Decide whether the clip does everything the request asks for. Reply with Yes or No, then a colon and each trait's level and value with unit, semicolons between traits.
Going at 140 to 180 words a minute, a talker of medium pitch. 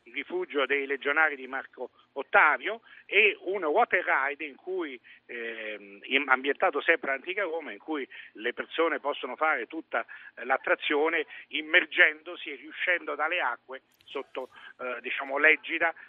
No: average, 130 wpm; medium, 160 Hz